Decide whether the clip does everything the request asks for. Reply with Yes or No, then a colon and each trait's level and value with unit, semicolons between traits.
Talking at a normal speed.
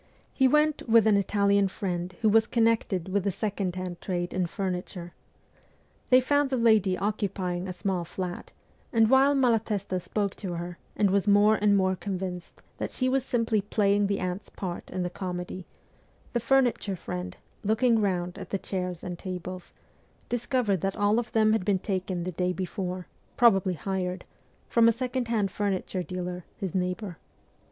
Yes: average, 170 wpm